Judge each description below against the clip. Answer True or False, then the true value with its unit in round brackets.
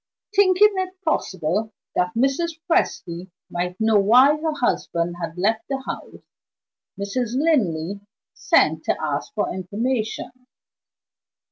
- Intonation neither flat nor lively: False (8.8 semitones)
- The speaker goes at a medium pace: False (115 wpm)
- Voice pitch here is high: True (225 Hz)